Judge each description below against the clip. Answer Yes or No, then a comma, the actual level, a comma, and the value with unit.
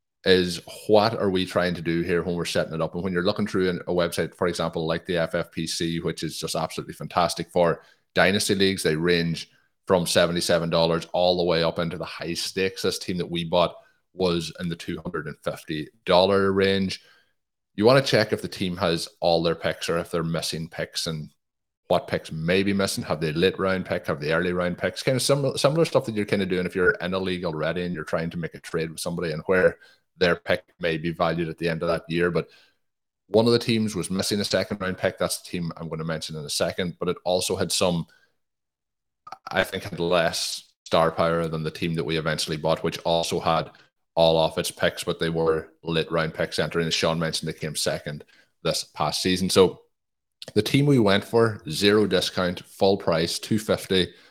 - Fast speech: Yes, fast, 220 wpm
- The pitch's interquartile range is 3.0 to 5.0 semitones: No, narrow, 2.4 semitones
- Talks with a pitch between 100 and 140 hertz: No, very low, 85 Hz